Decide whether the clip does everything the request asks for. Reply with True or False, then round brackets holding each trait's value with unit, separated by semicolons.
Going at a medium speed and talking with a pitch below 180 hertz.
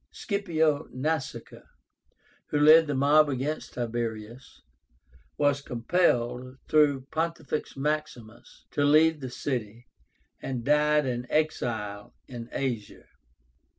False (100 wpm; 140 Hz)